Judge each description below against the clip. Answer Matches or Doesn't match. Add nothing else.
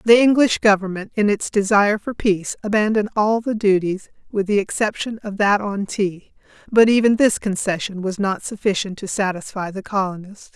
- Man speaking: Doesn't match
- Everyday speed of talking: Matches